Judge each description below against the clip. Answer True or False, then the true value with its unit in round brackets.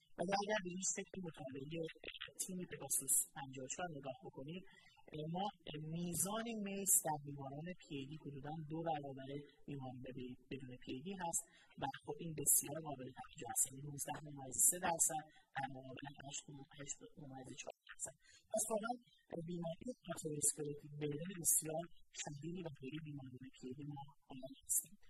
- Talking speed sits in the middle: True (120 wpm)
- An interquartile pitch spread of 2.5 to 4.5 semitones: True (3.9 semitones)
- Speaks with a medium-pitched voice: True (150 Hz)